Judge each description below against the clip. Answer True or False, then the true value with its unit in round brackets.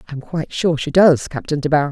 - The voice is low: False (150 Hz)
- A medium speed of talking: False (250 wpm)